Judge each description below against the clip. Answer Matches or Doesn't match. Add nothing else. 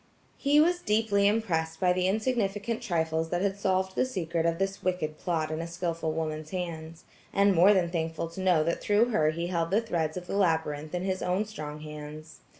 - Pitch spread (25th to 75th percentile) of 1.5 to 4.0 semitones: Matches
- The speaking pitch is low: Doesn't match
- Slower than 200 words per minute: Doesn't match